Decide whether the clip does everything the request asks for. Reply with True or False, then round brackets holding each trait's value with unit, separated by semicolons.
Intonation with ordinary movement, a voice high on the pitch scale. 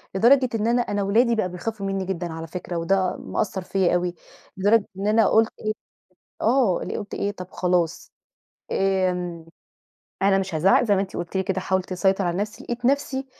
True (3.2 semitones; 195 Hz)